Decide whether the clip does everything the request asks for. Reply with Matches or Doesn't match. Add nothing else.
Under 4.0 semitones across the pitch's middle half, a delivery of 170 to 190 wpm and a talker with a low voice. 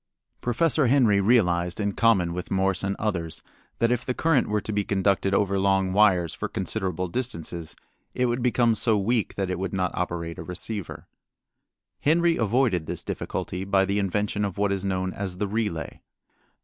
Matches